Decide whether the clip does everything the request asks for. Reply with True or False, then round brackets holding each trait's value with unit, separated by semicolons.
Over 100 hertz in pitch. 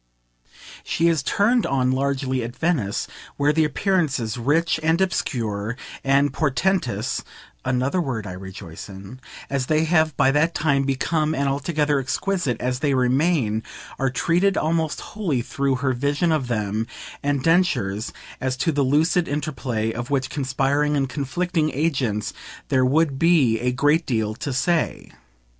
True (140 Hz)